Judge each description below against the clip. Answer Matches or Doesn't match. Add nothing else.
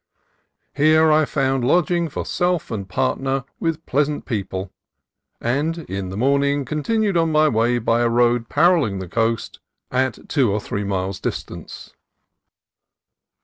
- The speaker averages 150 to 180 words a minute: Doesn't match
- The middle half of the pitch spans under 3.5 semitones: Doesn't match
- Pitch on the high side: Doesn't match